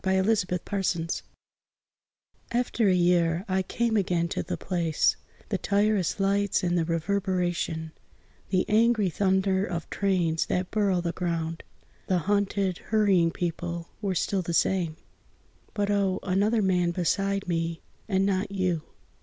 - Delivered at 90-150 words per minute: Yes, average, 140 wpm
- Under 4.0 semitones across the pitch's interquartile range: Yes, narrow, 2.6 semitones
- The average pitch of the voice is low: No, medium, 185 Hz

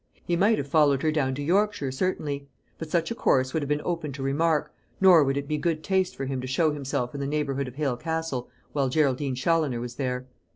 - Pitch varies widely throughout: No, average, 3.3 semitones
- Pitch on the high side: No, medium, 145 Hz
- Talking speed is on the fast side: Yes, fast, 235 wpm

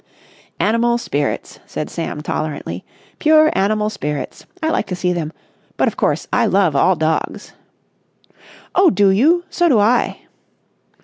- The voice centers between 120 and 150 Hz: No, high, 205 Hz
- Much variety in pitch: Yes, wide, 7.7 semitones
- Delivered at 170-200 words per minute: No, average, 140 wpm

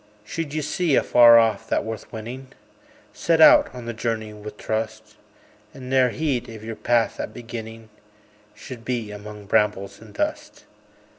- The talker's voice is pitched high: No, low, 115 Hz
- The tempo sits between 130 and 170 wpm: Yes, average, 155 wpm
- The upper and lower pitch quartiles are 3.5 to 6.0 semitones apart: No, narrow, 2.6 semitones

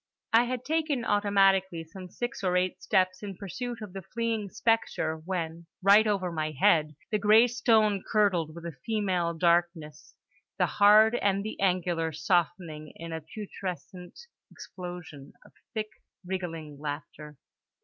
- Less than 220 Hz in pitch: Yes, medium, 185 Hz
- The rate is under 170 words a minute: Yes, average, 140 wpm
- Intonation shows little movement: No, average, 4.2 semitones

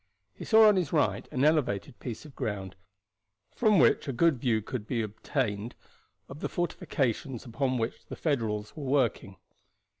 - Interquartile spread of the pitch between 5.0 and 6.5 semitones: Yes, wide, 5.4 semitones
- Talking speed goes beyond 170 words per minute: No, average, 160 wpm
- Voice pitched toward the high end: No, low, 130 Hz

